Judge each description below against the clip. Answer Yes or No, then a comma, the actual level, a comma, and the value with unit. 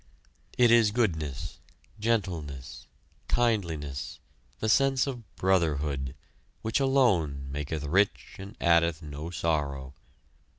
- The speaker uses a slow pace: Yes, slow, 95 wpm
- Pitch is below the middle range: Yes, very low, 85 Hz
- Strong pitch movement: Yes, wide, 7.2 semitones